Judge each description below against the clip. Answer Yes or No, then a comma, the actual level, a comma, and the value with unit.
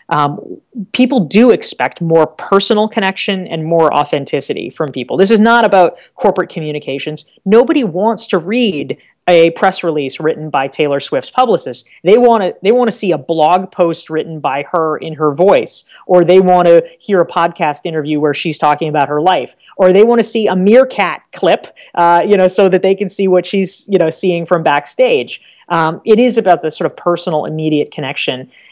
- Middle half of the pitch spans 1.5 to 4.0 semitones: No, average, 4.4 semitones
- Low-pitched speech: No, medium, 180 Hz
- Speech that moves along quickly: No, average, 190 wpm